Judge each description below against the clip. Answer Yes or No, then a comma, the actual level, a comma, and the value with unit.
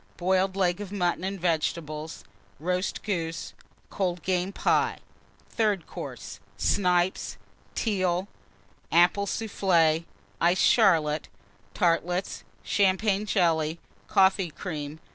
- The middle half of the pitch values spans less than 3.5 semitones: Yes, average, 2.8 semitones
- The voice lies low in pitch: No, medium, 180 Hz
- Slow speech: Yes, slow, 95 wpm